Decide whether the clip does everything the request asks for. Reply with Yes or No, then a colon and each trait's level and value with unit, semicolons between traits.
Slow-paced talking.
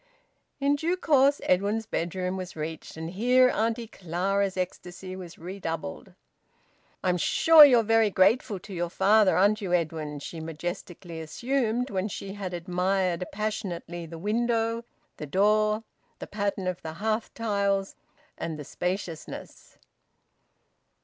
Yes: slow, 130 wpm